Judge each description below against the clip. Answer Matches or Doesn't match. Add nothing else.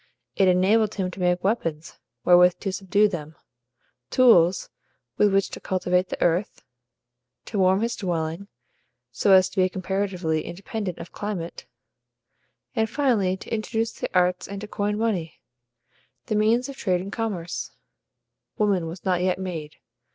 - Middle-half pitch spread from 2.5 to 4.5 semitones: Matches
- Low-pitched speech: Doesn't match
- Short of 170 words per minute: Matches